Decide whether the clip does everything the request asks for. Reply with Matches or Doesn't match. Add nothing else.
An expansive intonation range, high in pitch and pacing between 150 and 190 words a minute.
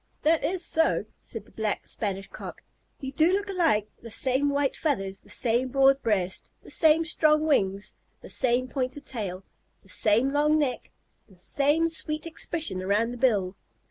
Matches